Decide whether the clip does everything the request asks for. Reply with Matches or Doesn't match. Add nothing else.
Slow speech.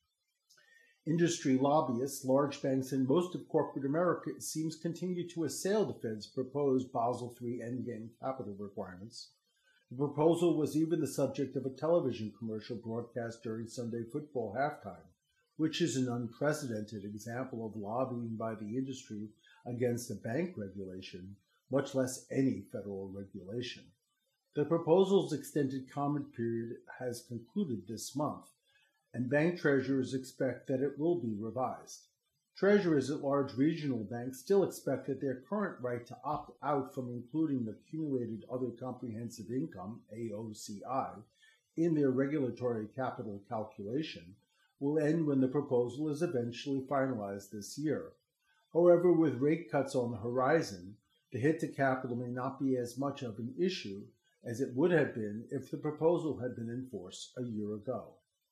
Doesn't match